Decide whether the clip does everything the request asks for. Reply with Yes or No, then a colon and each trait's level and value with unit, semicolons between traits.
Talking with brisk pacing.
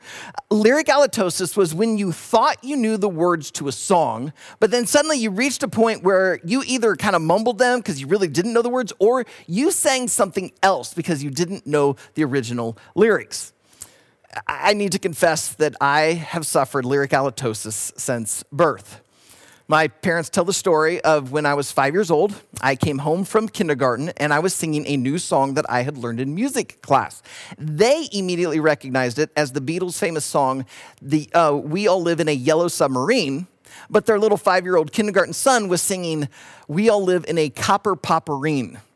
No: average, 190 wpm